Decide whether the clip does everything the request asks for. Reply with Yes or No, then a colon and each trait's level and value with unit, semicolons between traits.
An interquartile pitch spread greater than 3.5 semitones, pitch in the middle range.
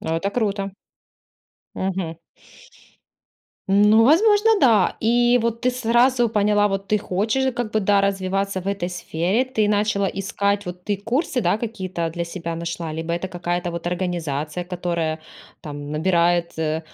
No: average, 4.0 semitones; high, 195 Hz